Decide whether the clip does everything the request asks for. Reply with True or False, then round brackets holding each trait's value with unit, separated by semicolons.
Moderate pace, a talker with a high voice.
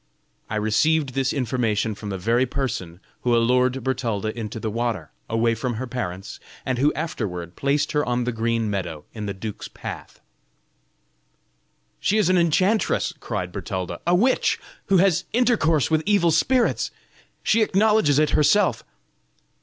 False (150 wpm; 125 Hz)